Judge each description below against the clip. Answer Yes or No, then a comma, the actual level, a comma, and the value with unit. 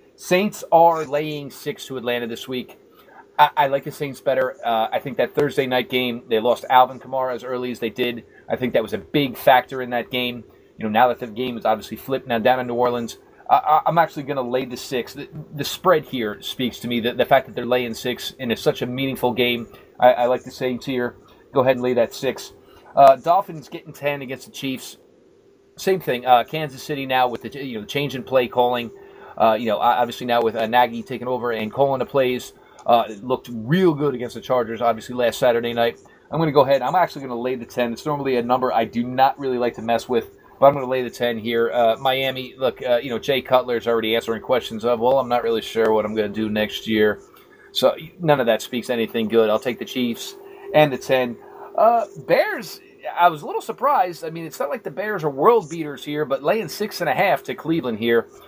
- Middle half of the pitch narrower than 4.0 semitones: Yes, average, 3.5 semitones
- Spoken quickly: Yes, fast, 245 wpm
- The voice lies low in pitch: Yes, low, 125 Hz